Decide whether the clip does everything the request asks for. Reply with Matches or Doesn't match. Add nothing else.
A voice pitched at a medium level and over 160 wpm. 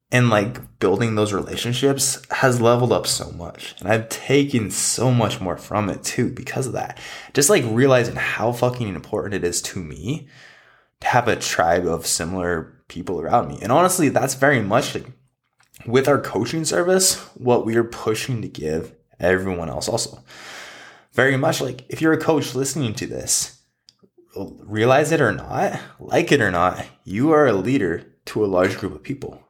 Doesn't match